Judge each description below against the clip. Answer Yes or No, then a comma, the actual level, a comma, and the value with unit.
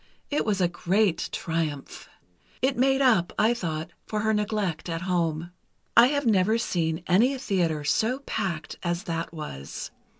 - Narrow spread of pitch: No, average, 5.3 semitones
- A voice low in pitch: No, medium, 185 Hz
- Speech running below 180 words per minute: Yes, average, 155 wpm